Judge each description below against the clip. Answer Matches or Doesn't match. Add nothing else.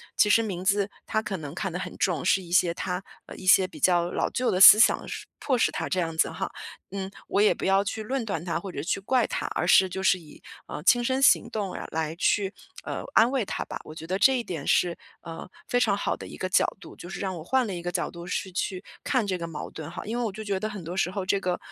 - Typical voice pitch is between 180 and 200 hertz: Matches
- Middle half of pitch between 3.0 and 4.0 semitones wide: Matches